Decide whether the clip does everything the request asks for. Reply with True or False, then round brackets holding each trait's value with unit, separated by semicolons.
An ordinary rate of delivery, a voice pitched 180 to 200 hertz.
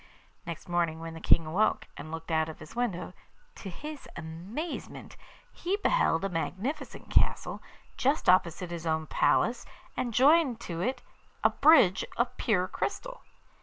True (150 wpm; 185 Hz)